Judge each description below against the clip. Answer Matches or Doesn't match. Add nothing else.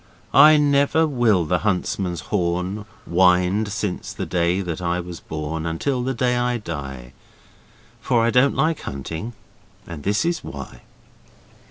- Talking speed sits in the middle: Matches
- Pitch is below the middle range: Matches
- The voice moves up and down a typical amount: Doesn't match